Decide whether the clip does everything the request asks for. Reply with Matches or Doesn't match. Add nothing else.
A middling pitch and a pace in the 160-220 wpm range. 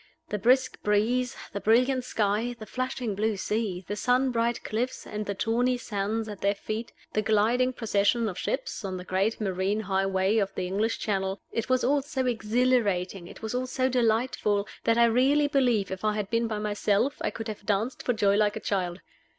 Doesn't match